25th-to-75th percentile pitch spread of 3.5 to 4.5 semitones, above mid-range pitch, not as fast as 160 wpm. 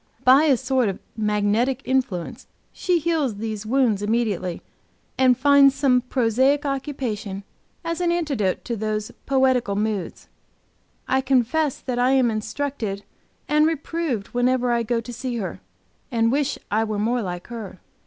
Yes: average, 4.0 semitones; high, 245 Hz; average, 145 wpm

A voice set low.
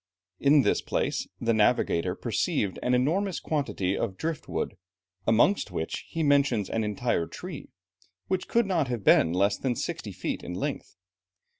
Yes: low, 120 Hz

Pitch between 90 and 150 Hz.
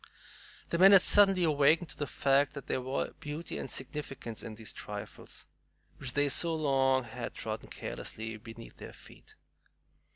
Yes: medium, 140 Hz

